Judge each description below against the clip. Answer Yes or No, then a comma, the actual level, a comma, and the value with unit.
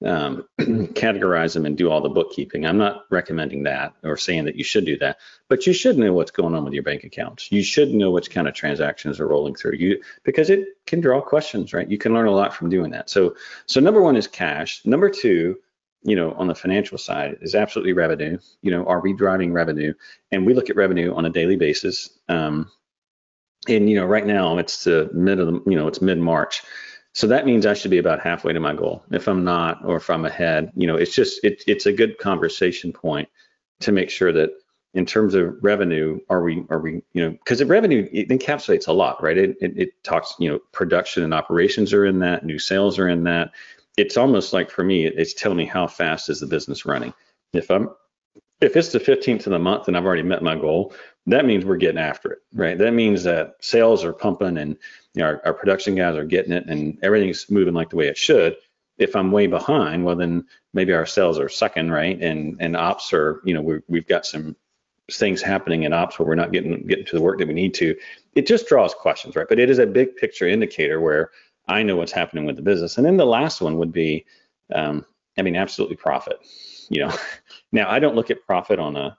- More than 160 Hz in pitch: No, very low, 95 Hz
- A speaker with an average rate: No, fast, 235 wpm